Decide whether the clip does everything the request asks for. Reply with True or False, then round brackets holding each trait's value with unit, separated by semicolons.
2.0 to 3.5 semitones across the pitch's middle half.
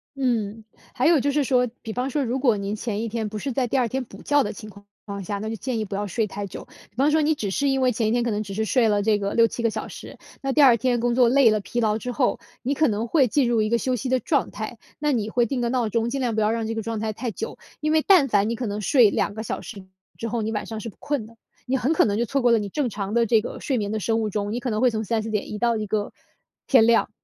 True (3.1 semitones)